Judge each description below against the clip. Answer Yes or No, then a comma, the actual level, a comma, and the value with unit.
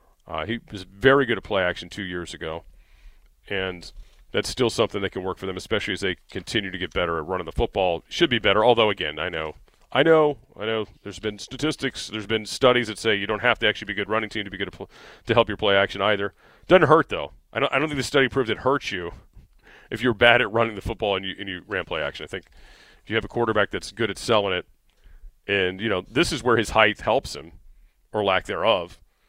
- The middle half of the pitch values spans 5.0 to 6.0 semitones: No, average, 3.9 semitones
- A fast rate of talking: Yes, fast, 255 wpm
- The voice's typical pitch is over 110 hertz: No, low, 105 Hz